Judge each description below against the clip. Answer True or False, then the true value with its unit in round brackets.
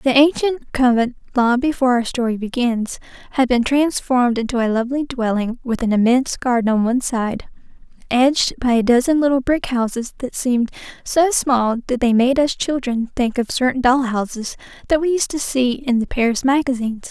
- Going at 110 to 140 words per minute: False (180 wpm)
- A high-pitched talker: True (250 Hz)